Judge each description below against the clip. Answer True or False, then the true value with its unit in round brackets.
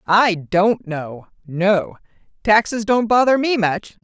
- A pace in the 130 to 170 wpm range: True (135 wpm)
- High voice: True (200 Hz)